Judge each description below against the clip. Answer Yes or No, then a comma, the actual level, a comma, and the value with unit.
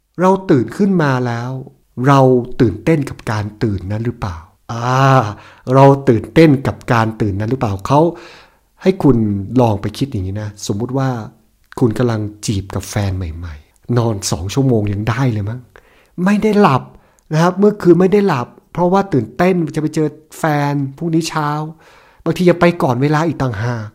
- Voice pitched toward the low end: Yes, low, 130 Hz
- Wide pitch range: Yes, wide, 6.5 semitones